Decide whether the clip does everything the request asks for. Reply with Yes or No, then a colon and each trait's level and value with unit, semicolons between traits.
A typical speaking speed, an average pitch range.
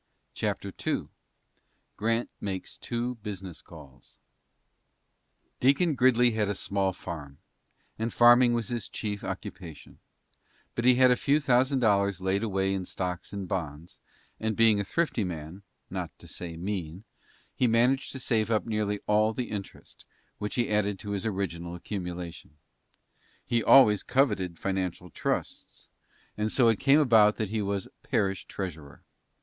Yes: average, 145 wpm; average, 4.2 semitones